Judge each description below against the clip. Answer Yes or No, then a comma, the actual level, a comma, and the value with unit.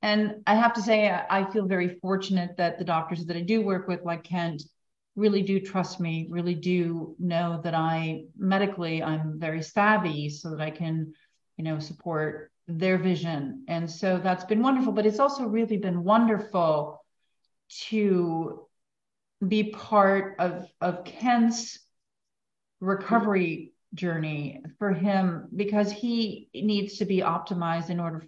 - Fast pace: No, average, 150 wpm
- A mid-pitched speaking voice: Yes, medium, 180 Hz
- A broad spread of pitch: No, average, 3.9 semitones